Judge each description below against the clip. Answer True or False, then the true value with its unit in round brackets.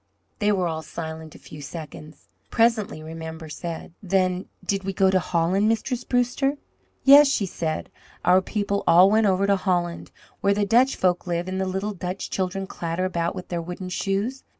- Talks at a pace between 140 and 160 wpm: False (180 wpm)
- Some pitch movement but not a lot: True (3.1 semitones)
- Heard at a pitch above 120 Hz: True (185 Hz)